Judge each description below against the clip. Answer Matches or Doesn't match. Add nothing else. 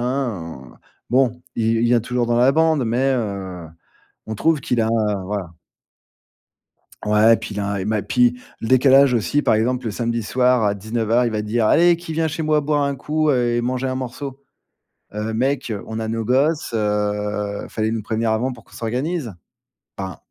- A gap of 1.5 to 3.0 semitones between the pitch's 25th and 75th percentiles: Doesn't match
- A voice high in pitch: Doesn't match